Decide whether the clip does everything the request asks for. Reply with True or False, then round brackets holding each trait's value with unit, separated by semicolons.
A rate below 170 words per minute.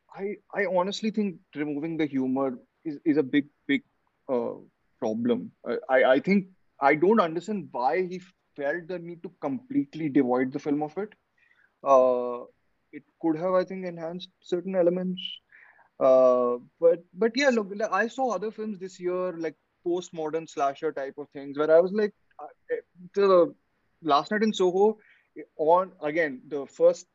True (160 wpm)